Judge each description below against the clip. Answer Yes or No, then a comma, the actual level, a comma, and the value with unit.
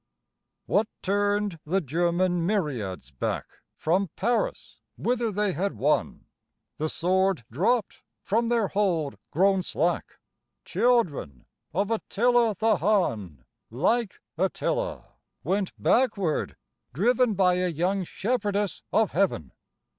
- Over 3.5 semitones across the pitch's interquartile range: Yes, average, 4.3 semitones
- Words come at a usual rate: No, slow, 110 wpm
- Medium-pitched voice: No, high, 195 Hz